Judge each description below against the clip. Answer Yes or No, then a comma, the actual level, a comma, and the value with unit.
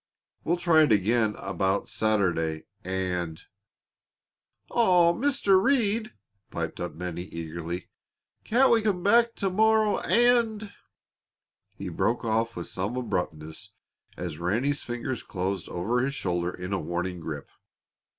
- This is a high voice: No, low, 110 Hz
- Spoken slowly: Yes, slow, 130 wpm